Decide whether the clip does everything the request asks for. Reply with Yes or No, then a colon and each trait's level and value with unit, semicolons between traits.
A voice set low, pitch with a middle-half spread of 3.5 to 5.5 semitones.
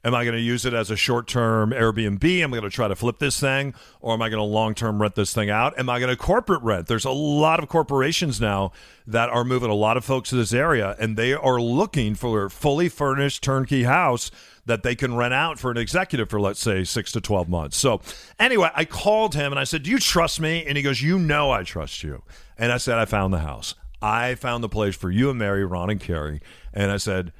Yes: low, 120 Hz; average, 4.5 semitones